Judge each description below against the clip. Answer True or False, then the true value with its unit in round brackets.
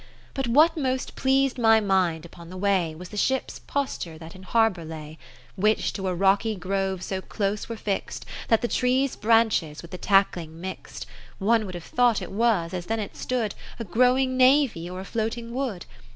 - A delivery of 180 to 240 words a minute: True (195 wpm)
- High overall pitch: True (205 Hz)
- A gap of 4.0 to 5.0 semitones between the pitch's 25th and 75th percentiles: True (4.7 semitones)